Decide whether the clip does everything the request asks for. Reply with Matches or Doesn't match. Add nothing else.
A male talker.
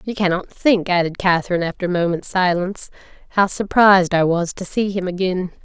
Doesn't match